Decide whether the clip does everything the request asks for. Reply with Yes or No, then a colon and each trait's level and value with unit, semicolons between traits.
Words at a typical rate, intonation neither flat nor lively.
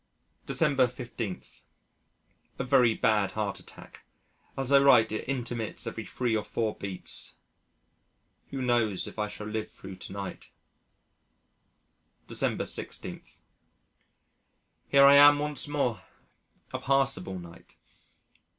No: slow, 115 wpm; average, 4.4 semitones